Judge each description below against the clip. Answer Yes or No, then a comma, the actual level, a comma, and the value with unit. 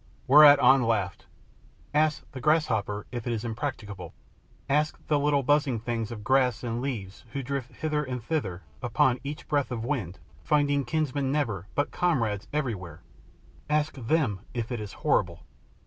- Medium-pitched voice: No, low, 130 Hz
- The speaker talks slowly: No, average, 155 wpm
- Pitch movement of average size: Yes, average, 4.7 semitones